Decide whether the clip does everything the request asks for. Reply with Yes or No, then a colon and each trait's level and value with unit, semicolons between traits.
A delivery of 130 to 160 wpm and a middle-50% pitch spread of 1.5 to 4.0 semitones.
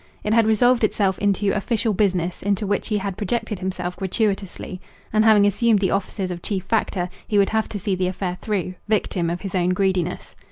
No: average, 200 wpm; narrow, 2.5 semitones